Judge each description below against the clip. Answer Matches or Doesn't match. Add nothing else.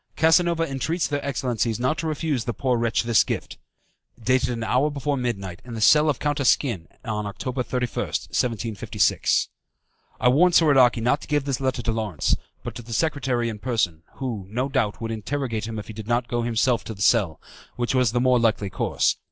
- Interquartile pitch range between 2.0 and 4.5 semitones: Matches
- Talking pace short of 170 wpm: Doesn't match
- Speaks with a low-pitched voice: Matches